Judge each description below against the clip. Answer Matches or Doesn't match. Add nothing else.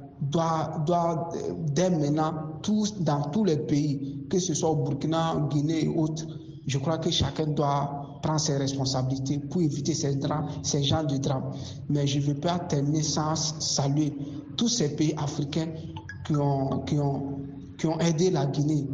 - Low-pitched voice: Doesn't match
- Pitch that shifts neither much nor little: Doesn't match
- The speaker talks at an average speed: Matches